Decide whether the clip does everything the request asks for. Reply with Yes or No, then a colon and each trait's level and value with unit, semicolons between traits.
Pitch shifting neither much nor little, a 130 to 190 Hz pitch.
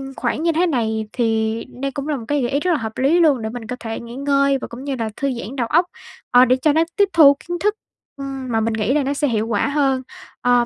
No: average, 3.8 semitones; very high, 265 Hz